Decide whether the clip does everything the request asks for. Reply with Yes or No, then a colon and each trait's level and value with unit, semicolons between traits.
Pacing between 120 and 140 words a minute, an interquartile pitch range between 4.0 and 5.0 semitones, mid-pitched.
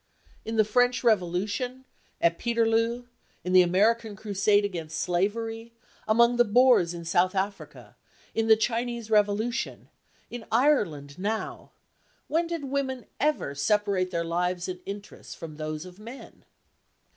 No: slow, 135 wpm; average, 4.5 semitones; high, 210 Hz